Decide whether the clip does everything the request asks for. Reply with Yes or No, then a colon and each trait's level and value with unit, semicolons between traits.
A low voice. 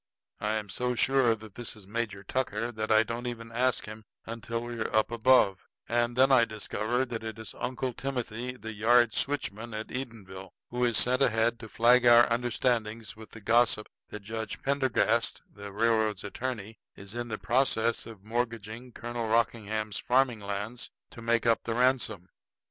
Yes: low, 115 Hz